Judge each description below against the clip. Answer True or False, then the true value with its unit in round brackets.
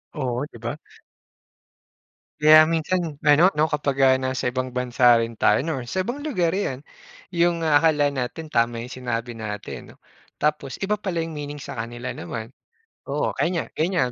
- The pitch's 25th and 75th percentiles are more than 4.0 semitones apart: True (4.9 semitones)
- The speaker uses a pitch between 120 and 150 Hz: True (140 Hz)